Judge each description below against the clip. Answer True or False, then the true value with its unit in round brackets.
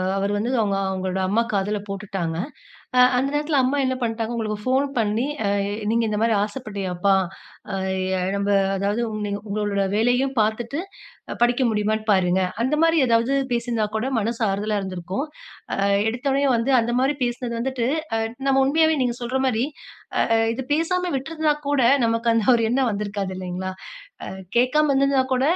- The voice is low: False (230 Hz)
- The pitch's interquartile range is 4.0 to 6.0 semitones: True (4.4 semitones)